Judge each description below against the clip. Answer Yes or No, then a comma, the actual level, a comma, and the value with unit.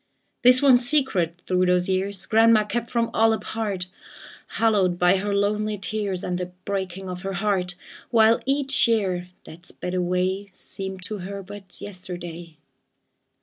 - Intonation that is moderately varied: Yes, average, 3.3 semitones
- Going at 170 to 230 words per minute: No, average, 145 wpm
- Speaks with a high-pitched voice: Yes, high, 195 Hz